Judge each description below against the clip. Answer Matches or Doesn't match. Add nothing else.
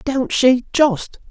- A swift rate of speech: Doesn't match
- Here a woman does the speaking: Doesn't match